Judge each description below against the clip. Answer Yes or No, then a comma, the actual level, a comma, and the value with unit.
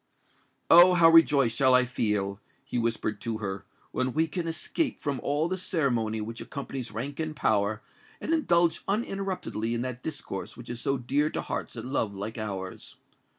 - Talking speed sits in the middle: Yes, average, 175 wpm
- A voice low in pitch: Yes, low, 130 Hz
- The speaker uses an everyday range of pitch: No, wide, 6.4 semitones